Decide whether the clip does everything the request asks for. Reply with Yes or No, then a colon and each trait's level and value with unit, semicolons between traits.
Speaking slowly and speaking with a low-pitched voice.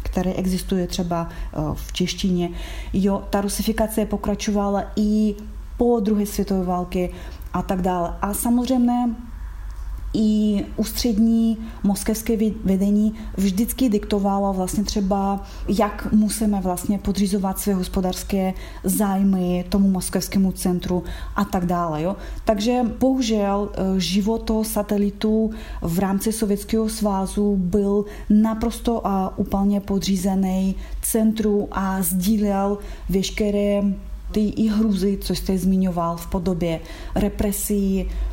No: slow, 105 wpm; high, 200 Hz